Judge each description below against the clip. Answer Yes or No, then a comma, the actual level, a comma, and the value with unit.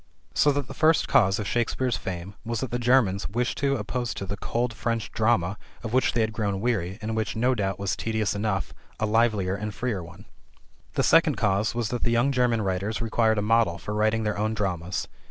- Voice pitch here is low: Yes, low, 110 Hz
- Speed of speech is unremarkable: No, fast, 215 wpm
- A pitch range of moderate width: Yes, average, 3.0 semitones